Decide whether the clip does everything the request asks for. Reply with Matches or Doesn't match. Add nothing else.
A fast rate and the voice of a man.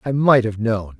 Matches